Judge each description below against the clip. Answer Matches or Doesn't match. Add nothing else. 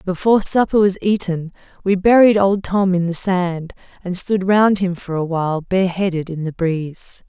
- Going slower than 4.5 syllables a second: Doesn't match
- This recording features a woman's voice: Matches